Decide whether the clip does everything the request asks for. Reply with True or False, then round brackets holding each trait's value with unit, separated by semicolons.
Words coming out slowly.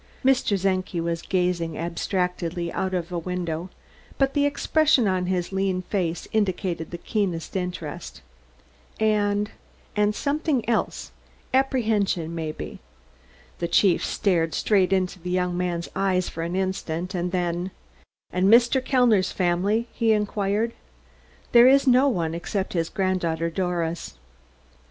True (130 wpm)